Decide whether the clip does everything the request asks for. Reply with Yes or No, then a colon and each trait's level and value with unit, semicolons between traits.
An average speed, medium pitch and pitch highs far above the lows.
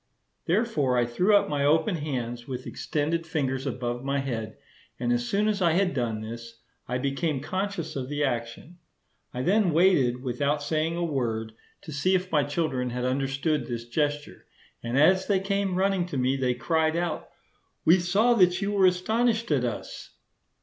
Yes: average, 175 wpm; medium, 145 Hz; wide, 6.2 semitones